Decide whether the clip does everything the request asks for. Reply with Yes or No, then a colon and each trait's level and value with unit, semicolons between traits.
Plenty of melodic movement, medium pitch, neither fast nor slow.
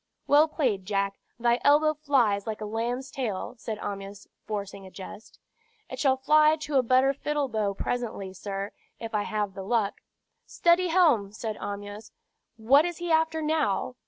No: wide, 6.4 semitones; high, 235 Hz; average, 170 wpm